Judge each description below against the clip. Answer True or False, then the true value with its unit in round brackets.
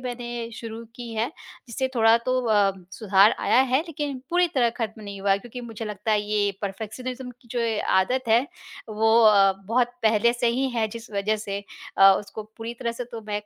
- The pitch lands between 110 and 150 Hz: False (225 Hz)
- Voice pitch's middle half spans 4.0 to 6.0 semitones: False (2.6 semitones)